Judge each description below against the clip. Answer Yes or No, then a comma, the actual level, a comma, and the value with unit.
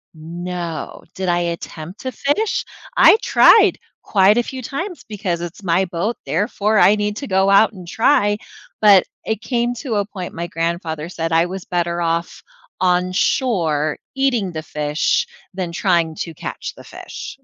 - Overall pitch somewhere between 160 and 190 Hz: Yes, medium, 185 Hz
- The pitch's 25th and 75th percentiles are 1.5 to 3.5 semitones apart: No, average, 4.0 semitones